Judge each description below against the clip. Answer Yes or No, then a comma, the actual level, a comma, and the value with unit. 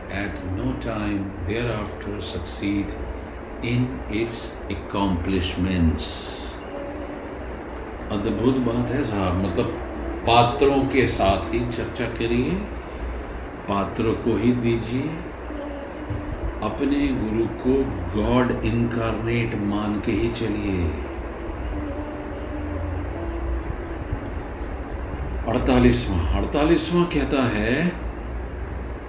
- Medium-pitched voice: No, low, 100 Hz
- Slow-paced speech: Yes, slow, 75 wpm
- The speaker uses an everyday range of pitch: No, wide, 6.1 semitones